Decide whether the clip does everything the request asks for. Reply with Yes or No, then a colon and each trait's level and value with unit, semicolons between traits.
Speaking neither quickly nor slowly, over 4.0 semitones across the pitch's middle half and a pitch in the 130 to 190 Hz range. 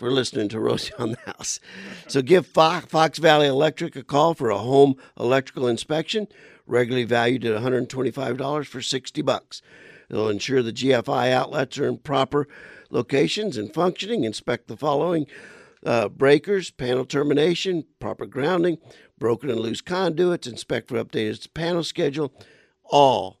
Yes: average, 150 wpm; average, 4.5 semitones; medium, 140 Hz